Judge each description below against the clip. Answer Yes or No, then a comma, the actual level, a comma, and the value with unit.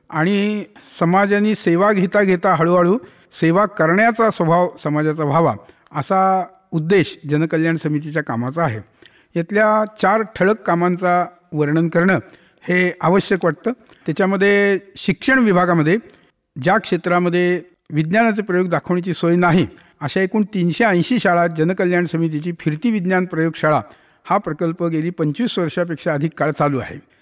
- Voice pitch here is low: No, medium, 175 Hz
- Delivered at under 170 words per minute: Yes, average, 120 wpm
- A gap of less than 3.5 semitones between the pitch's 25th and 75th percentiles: Yes, average, 3.1 semitones